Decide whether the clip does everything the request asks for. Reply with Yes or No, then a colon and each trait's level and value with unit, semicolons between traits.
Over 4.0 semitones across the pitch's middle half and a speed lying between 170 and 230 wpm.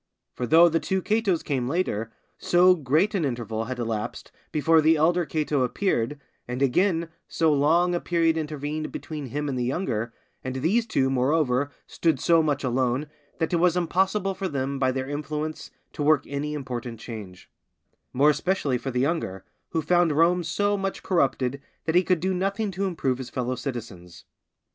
Yes: average, 5.2 semitones; average, 175 wpm